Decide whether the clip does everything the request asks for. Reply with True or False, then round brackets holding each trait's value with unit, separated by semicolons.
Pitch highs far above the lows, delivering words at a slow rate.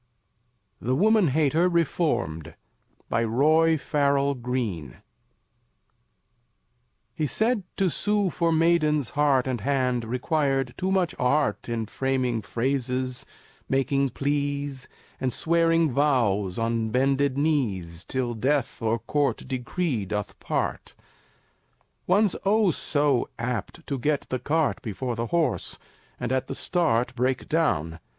False (4.6 semitones; 120 wpm)